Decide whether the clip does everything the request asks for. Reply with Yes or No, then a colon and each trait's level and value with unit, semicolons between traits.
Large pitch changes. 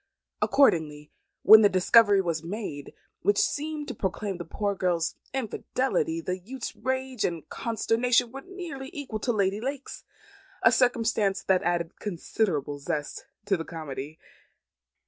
Yes: wide, 6.6 semitones